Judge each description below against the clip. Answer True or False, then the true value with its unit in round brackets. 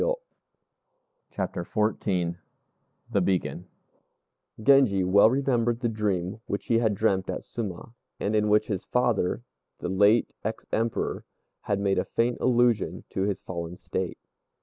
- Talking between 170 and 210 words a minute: False (140 wpm)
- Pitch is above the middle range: False (105 Hz)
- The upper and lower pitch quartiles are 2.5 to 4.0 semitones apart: True (3.6 semitones)